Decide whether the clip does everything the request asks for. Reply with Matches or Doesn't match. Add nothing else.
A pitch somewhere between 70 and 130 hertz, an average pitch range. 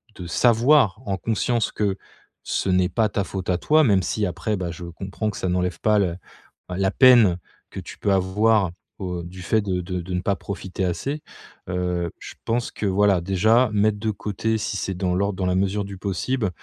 Matches